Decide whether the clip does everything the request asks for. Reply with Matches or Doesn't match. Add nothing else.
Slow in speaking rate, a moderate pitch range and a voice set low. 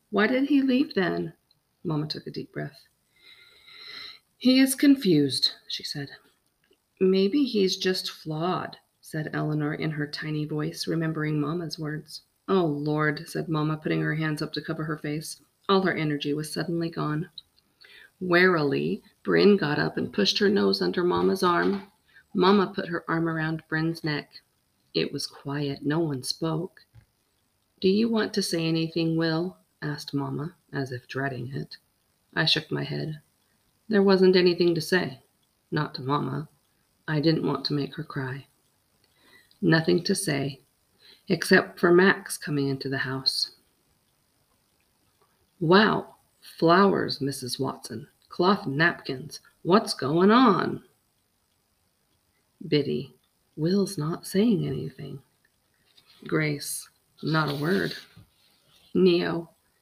Doesn't match